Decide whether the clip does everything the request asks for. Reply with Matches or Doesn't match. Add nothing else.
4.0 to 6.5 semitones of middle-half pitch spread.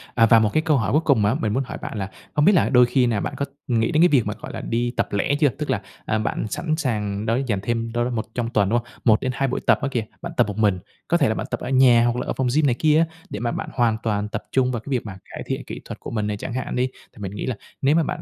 Doesn't match